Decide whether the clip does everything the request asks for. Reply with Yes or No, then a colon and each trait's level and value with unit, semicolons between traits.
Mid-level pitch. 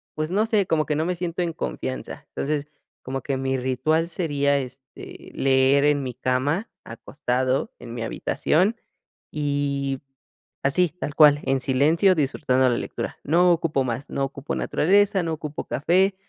Yes: medium, 145 Hz